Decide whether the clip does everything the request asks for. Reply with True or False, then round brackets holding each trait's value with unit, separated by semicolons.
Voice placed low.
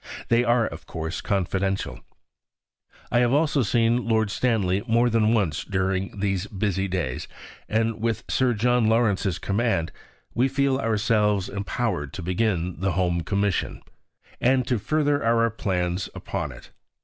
True (105 Hz)